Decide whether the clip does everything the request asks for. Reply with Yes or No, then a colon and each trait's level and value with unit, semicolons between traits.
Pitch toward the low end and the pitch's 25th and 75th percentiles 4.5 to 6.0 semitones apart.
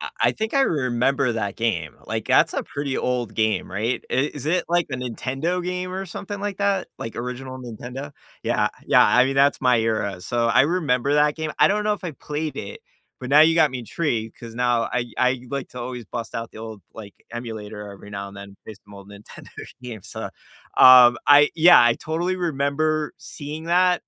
Yes: low, 130 Hz; wide, 5.4 semitones